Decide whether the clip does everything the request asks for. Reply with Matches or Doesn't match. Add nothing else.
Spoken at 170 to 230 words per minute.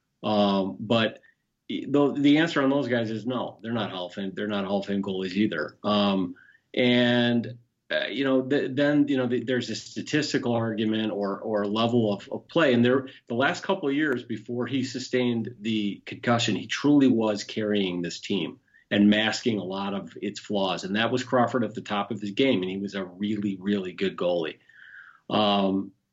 Matches